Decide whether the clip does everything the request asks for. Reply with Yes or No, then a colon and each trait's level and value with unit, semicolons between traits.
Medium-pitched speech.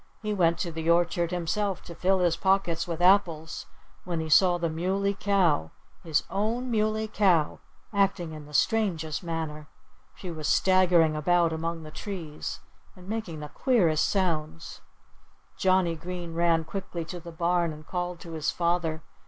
Yes: medium, 170 Hz